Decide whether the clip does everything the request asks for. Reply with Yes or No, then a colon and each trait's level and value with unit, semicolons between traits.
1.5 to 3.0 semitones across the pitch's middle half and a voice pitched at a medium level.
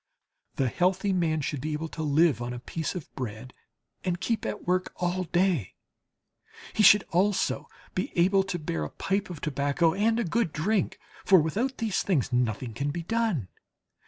No: average, 5.2 semitones; medium, 170 Hz